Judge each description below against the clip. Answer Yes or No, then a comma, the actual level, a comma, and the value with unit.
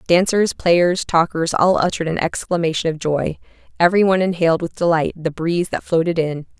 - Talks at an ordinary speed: Yes, average, 165 wpm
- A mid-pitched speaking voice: Yes, medium, 170 Hz